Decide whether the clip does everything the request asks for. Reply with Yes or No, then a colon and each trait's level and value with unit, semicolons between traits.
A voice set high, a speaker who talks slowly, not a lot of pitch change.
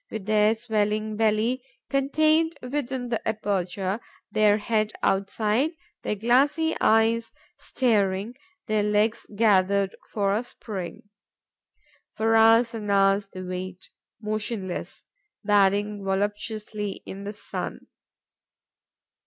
Yes: high, 215 Hz; slow, 105 wpm; narrow, 2.3 semitones